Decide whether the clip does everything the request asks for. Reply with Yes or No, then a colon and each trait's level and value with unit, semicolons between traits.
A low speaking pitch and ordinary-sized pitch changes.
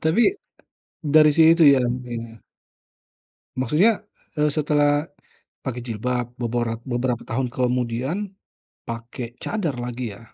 Yes: low, 125 Hz; average, 4.1 semitones